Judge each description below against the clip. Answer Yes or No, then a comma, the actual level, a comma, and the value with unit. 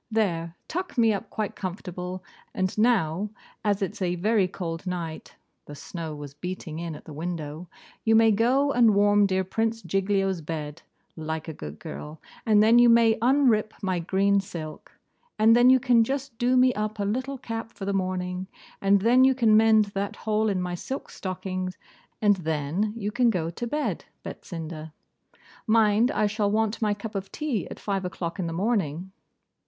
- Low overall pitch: No, high, 200 Hz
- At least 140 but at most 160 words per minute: No, average, 180 wpm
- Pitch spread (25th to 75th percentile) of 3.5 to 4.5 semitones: Yes, average, 4.2 semitones